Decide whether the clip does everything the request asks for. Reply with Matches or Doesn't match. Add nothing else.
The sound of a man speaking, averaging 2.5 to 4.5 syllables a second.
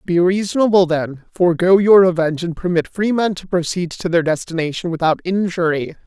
Doesn't match